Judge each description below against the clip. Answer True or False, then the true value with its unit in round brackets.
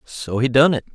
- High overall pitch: False (130 Hz)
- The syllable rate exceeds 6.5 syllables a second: False (5.1 syllables/s)